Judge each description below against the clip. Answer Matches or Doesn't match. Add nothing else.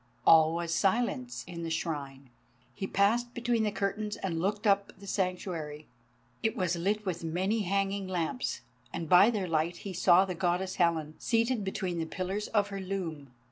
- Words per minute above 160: Matches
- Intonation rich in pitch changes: Doesn't match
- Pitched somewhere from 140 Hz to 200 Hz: Matches